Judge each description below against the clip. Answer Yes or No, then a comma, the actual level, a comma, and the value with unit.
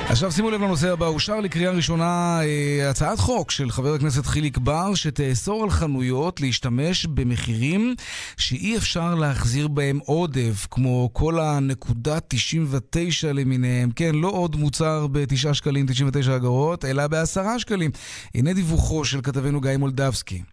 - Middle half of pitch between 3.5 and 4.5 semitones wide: Yes, average, 3.9 semitones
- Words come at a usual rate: Yes, average, 135 wpm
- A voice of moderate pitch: Yes, medium, 145 Hz